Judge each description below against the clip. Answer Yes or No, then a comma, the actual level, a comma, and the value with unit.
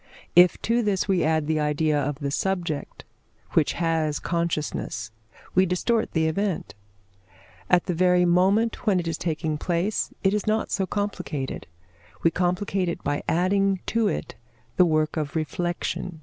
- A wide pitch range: No, average, 3.7 semitones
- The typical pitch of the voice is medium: Yes, medium, 175 Hz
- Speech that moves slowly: No, average, 155 wpm